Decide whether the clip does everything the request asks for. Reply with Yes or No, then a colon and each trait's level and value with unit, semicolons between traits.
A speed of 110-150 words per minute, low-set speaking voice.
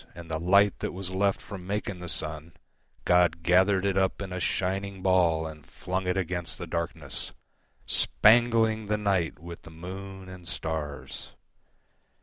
Yes: average, 140 wpm; very low, 90 Hz